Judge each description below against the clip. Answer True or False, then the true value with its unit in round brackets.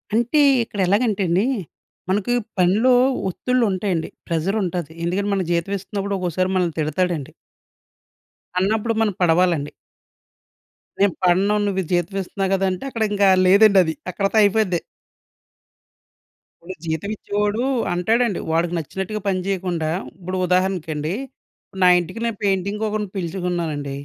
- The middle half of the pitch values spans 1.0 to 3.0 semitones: True (2.7 semitones)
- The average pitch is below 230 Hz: True (190 Hz)